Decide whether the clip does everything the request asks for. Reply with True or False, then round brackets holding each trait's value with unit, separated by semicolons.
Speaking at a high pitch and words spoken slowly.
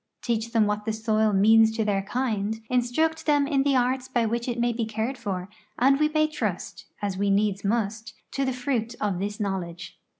False (225 Hz; 205 wpm)